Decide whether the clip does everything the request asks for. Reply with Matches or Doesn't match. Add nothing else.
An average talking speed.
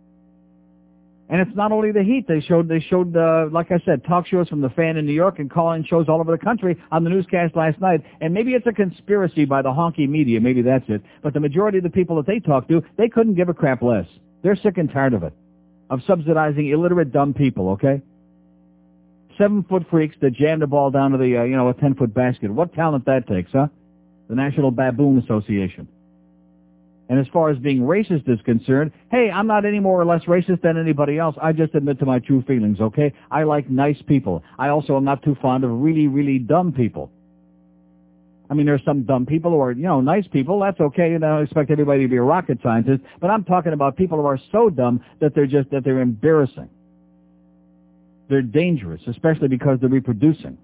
Doesn't match